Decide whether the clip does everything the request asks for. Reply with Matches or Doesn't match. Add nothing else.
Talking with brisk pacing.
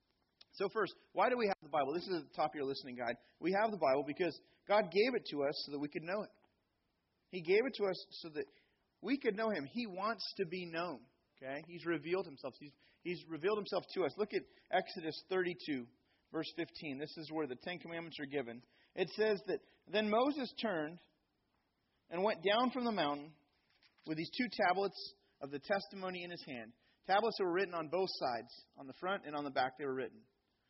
Matches